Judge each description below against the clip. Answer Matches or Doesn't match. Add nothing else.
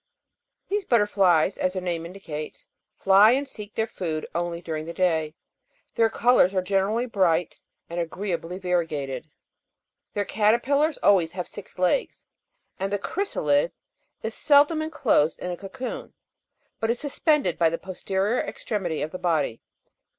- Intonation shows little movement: Doesn't match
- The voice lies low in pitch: Doesn't match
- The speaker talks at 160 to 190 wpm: Doesn't match